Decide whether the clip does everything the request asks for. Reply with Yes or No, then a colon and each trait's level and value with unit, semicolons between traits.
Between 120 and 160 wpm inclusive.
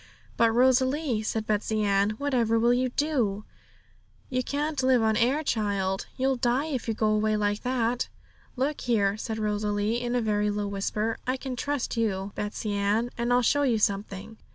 No: average, 175 wpm